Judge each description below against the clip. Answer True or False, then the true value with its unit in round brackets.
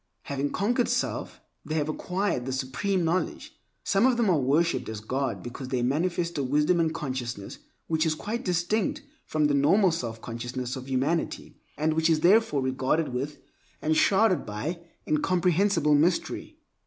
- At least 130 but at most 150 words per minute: False (165 wpm)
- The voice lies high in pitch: False (155 Hz)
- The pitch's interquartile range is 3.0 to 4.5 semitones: False (5.3 semitones)